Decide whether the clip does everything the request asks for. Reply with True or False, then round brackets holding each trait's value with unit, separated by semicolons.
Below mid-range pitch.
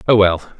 True (100 Hz)